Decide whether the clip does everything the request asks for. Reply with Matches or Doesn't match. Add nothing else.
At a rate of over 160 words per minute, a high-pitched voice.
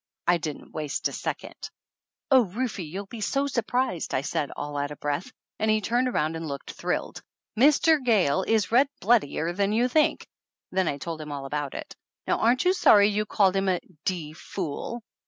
Matches